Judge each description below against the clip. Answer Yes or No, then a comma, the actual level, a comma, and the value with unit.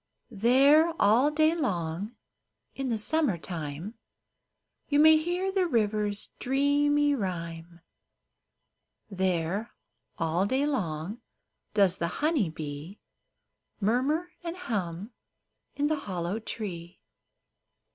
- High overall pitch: Yes, high, 215 Hz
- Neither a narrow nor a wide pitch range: No, wide, 9.0 semitones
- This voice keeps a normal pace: No, slow, 100 wpm